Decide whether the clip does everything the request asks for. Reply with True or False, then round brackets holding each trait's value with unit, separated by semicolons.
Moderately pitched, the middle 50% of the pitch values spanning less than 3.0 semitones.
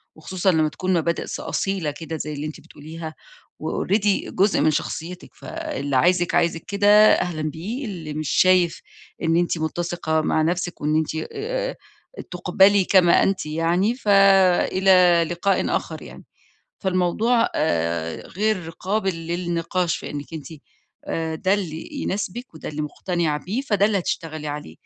False (175 Hz; 3.5 semitones)